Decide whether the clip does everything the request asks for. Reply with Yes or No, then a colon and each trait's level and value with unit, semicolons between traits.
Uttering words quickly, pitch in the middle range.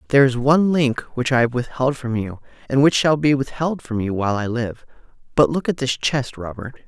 No: fast, 225 wpm; low, 130 Hz